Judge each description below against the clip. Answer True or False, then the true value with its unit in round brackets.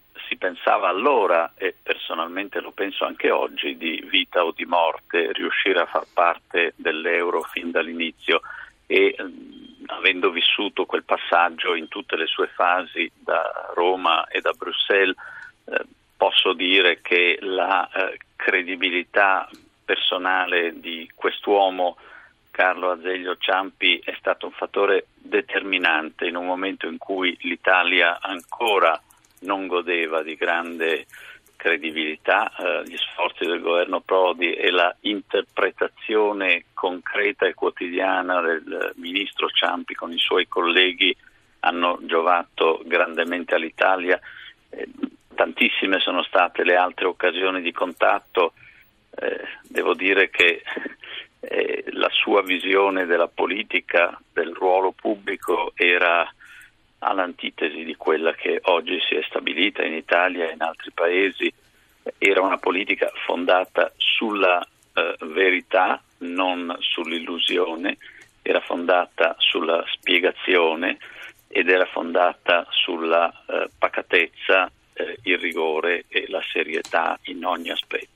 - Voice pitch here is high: True (345 Hz)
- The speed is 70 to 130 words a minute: True (120 wpm)